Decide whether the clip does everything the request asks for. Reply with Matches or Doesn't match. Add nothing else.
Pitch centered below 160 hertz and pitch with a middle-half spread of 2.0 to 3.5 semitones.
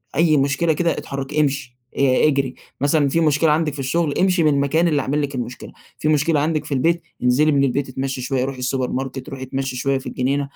Matches